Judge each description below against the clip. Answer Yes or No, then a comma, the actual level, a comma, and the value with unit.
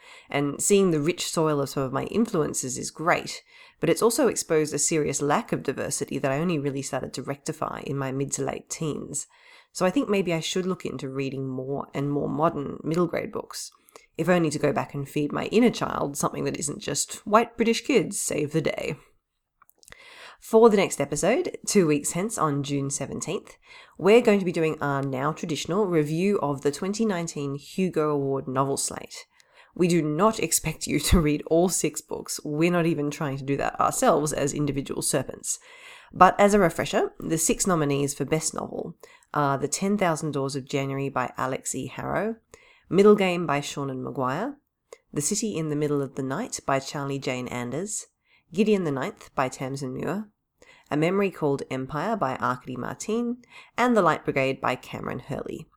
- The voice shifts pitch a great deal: Yes, wide, 6.7 semitones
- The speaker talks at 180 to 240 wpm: Yes, average, 190 wpm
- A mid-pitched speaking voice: Yes, medium, 155 Hz